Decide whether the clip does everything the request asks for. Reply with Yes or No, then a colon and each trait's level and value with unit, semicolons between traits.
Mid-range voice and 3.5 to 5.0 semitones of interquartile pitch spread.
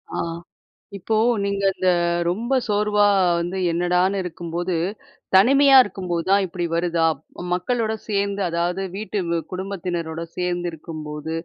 No: medium, 180 Hz; average, 2.9 semitones